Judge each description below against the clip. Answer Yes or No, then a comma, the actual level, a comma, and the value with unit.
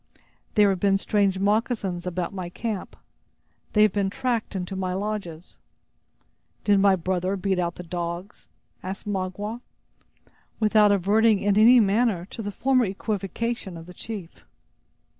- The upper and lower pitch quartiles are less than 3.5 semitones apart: Yes, average, 2.7 semitones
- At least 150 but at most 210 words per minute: No, average, 140 wpm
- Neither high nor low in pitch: No, high, 195 Hz